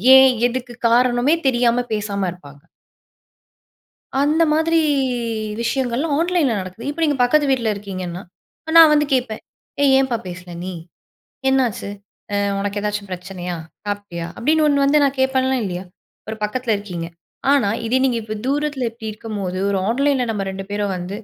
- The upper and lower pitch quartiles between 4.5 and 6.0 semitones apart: Yes, average, 5.1 semitones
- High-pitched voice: Yes, high, 235 Hz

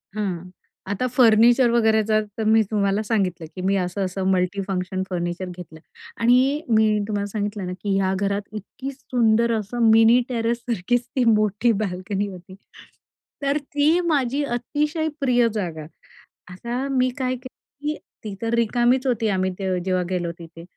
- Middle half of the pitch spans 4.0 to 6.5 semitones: Yes, average, 4.4 semitones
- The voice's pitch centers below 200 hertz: No, high, 215 Hz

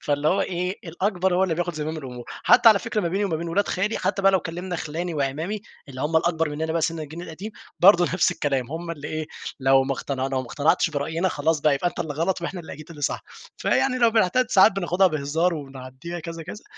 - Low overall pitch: No, medium, 165 Hz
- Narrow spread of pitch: No, average, 3.7 semitones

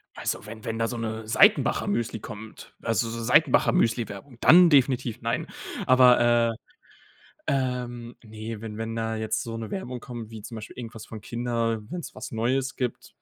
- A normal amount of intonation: No, narrow, 1.8 semitones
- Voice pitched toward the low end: Yes, low, 115 Hz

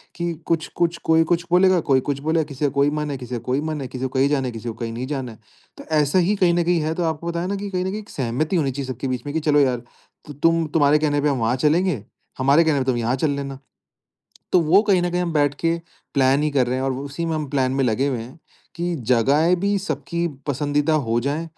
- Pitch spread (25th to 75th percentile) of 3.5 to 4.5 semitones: Yes, average, 4.1 semitones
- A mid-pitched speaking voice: Yes, medium, 145 Hz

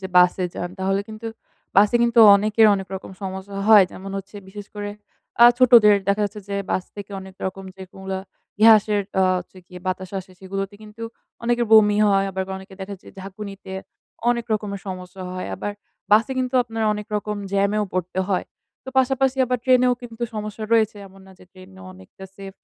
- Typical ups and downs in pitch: No, narrow, 2.3 semitones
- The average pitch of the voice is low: No, high, 200 Hz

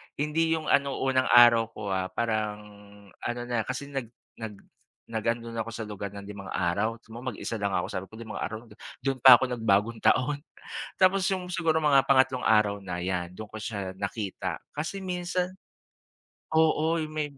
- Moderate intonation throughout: No, wide, 5.7 semitones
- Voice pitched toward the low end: Yes, low, 115 Hz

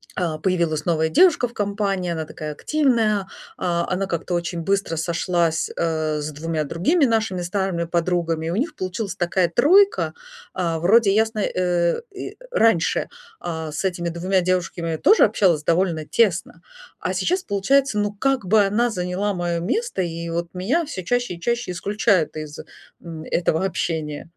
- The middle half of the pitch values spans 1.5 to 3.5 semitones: No, average, 3.9 semitones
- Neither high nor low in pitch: Yes, medium, 180 Hz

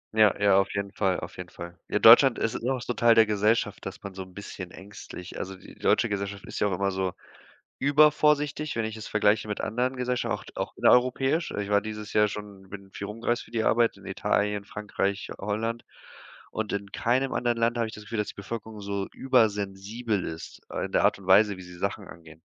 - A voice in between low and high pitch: No, low, 105 Hz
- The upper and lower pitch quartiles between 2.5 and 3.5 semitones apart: Yes, average, 2.9 semitones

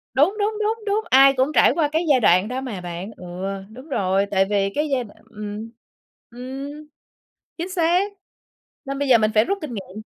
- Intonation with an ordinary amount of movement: No, wide, 6.8 semitones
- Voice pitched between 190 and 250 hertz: No, very high, 265 Hz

